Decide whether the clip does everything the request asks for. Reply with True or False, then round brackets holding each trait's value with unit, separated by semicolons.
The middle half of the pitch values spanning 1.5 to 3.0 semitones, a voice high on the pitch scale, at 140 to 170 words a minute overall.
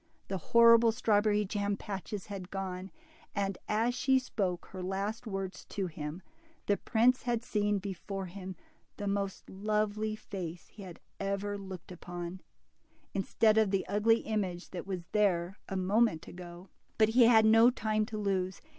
True (2.5 semitones; 200 Hz; 155 wpm)